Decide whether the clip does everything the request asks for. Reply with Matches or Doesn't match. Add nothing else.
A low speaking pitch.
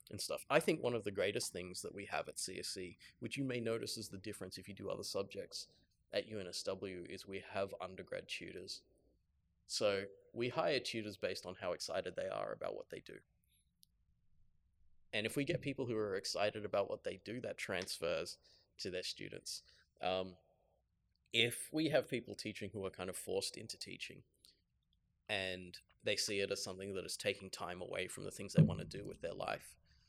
Matches